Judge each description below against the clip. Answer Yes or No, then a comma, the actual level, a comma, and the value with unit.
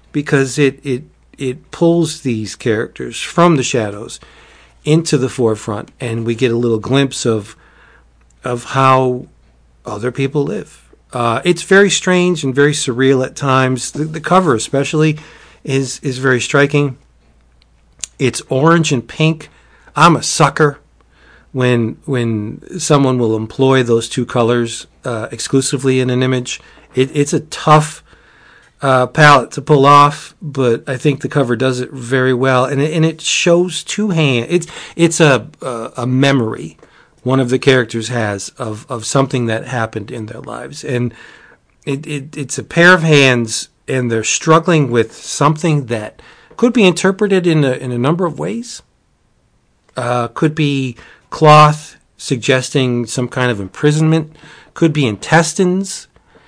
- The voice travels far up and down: No, average, 4.0 semitones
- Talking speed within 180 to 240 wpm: No, average, 150 wpm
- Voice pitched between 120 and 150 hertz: Yes, low, 135 Hz